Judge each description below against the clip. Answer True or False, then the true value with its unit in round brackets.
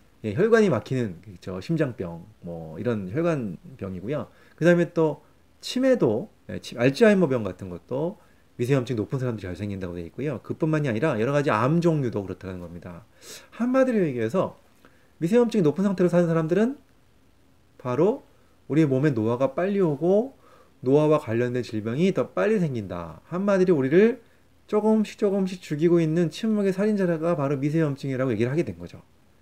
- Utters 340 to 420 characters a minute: True (360 characters per minute)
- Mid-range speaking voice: True (150 Hz)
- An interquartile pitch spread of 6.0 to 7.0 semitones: False (8.6 semitones)